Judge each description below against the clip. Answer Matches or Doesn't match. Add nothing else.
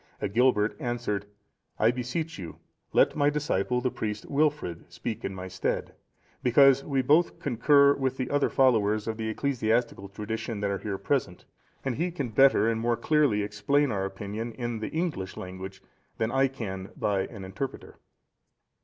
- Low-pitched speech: Matches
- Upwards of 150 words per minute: Matches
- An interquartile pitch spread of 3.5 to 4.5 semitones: Doesn't match